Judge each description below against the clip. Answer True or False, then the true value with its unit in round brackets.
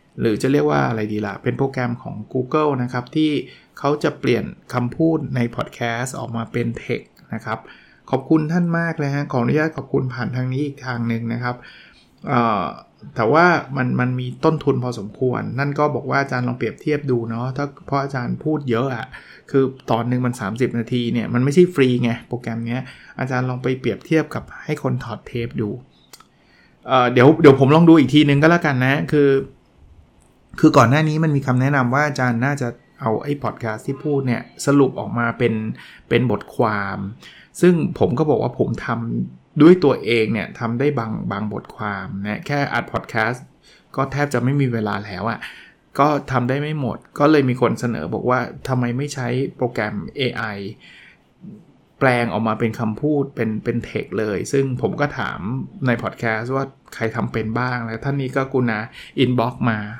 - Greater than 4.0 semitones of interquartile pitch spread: False (3.3 semitones)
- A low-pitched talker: True (125 Hz)